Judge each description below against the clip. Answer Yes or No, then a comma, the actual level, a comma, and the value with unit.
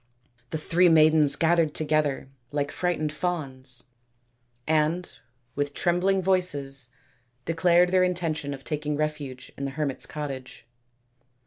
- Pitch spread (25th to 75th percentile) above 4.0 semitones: No, average, 3.5 semitones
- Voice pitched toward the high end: No, medium, 155 Hz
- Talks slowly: Yes, slow, 115 wpm